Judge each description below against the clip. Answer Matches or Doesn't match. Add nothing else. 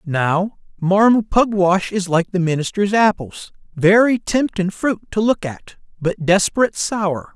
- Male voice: Matches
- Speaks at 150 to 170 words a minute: Doesn't match